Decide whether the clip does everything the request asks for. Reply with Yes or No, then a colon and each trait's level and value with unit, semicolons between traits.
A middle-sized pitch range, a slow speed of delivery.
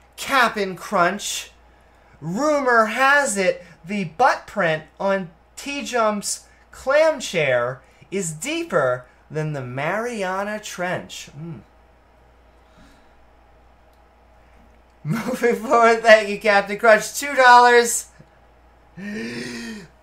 No: wide, 7.0 semitones; slow, 85 wpm